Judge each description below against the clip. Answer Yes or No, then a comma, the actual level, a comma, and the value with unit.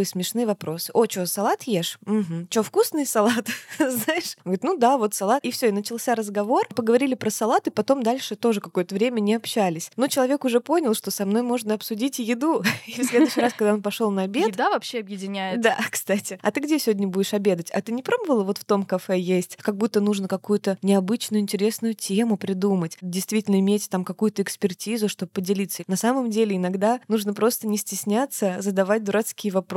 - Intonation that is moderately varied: Yes, average, 3.3 semitones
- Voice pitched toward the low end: No, high, 210 Hz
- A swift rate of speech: Yes, fast, 200 wpm